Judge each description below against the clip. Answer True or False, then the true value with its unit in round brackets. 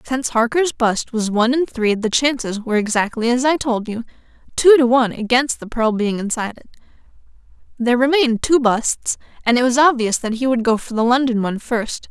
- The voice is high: True (240 Hz)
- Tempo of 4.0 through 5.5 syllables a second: False (5.7 syllables/s)